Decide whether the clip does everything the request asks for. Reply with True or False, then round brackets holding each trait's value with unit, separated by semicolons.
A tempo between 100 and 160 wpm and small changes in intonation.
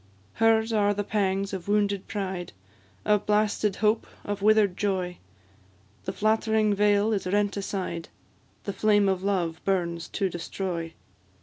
True (135 wpm; 1.9 semitones)